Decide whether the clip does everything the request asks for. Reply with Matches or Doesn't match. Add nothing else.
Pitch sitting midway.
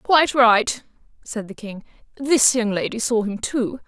Doesn't match